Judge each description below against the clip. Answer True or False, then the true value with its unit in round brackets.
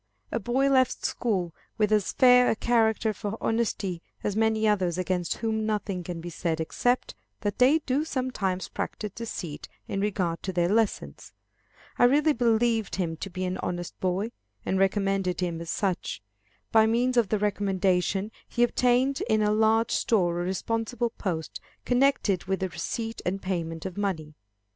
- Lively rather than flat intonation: False (4.0 semitones)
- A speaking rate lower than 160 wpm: False (165 wpm)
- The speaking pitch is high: True (205 Hz)